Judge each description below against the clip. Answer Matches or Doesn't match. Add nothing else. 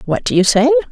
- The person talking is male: Doesn't match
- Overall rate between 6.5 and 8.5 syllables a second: Matches